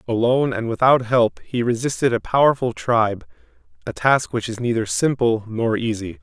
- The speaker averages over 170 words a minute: No, average, 165 wpm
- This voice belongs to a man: Yes, male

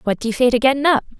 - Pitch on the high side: Yes, very high, 250 Hz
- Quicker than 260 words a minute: Yes, fast, 350 wpm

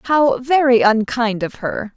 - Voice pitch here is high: Yes, high, 240 Hz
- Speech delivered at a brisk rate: No, average, 155 wpm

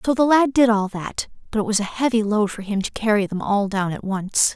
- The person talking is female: Yes, female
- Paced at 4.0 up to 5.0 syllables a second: No, 5.4 syllables/s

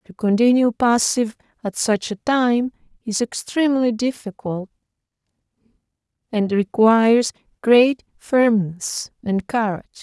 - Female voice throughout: Yes, female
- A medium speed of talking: No, slow, 95 wpm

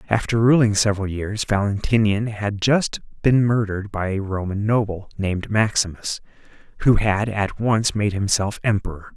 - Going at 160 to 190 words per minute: No, average, 145 wpm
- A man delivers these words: Yes, male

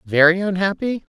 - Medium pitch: Yes, medium, 180 Hz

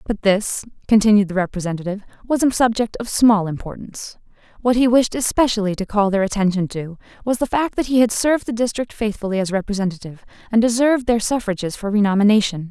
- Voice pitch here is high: Yes, high, 215 Hz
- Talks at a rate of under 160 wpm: No, average, 180 wpm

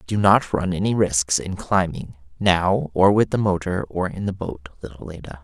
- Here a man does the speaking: Yes, male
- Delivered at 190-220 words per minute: Yes, average, 200 wpm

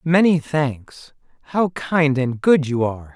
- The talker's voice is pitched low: No, medium, 145 Hz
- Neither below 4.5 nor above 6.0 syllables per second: No, 3.8 syllables/s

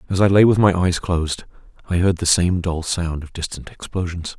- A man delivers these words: Yes, male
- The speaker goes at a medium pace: No, fast, 220 wpm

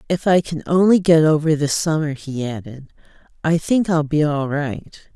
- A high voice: No, medium, 155 Hz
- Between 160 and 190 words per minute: Yes, average, 185 wpm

